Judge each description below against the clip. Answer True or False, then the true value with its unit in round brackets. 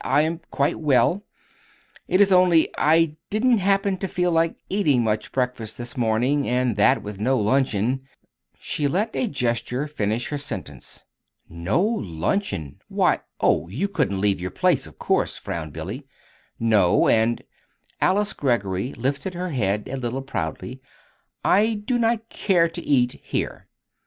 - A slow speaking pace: False (150 wpm)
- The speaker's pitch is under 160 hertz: True (135 Hz)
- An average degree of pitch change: False (8.5 semitones)